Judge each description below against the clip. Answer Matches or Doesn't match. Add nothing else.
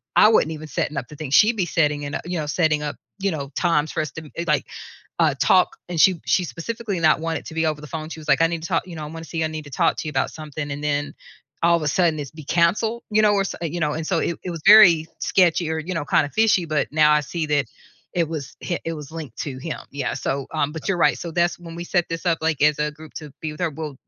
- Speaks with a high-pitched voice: Doesn't match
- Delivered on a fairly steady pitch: Matches